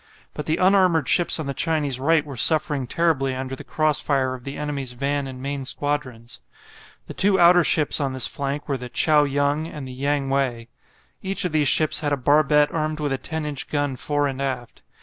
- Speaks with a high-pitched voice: No, medium, 145 Hz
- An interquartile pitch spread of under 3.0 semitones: Yes, narrow, 2.5 semitones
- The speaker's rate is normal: No, fast, 210 wpm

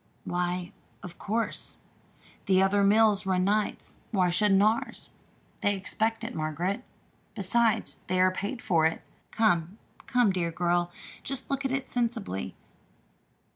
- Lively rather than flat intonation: No, average, 3.8 semitones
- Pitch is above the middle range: Yes, high, 195 Hz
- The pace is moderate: No, slow, 130 wpm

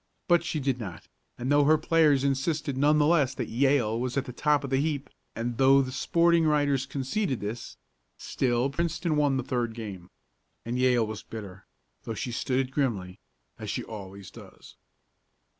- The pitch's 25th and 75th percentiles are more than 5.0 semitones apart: No, average, 3.9 semitones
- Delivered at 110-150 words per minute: No, average, 180 wpm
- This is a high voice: No, low, 135 Hz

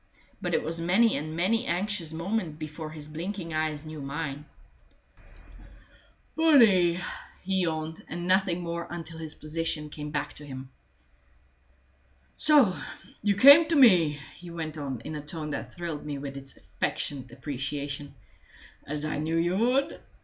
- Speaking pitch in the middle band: Yes, medium, 160 Hz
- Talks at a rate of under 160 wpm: Yes, average, 150 wpm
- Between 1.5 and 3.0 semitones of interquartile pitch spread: No, average, 3.5 semitones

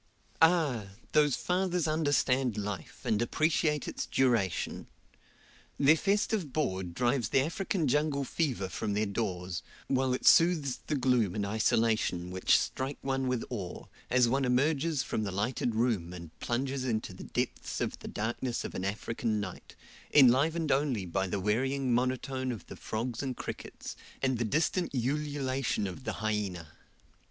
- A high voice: No, low, 125 Hz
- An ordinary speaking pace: Yes, average, 150 wpm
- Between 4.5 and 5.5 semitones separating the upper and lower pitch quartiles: Yes, average, 5.1 semitones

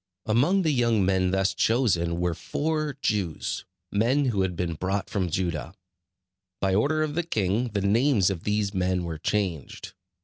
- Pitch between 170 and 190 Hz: No, low, 100 Hz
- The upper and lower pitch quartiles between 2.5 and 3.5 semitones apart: No, average, 5.1 semitones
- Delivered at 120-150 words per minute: No, average, 165 wpm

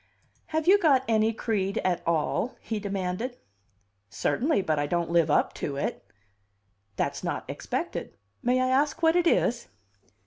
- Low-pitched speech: No, high, 225 Hz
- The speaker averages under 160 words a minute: Yes, average, 150 wpm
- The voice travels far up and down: Yes, wide, 7.1 semitones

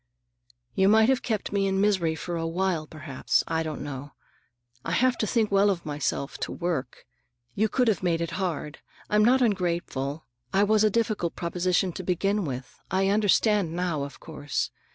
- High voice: No, medium, 180 Hz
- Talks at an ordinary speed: Yes, average, 180 wpm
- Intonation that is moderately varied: Yes, average, 4.4 semitones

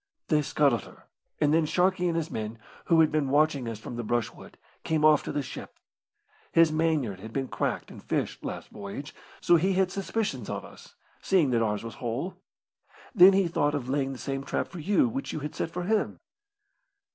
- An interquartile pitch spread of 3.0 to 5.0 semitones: No, wide, 5.6 semitones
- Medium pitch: Yes, medium, 150 Hz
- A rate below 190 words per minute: No, fast, 205 wpm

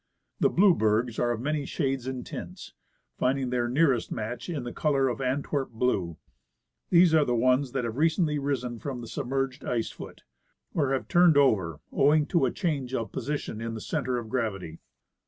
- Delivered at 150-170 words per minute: No, average, 180 wpm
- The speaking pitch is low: Yes, low, 130 Hz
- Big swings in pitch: No, average, 3.3 semitones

